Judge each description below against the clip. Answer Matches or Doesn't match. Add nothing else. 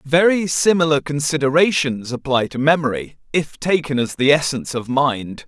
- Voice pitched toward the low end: Doesn't match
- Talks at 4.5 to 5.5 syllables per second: Matches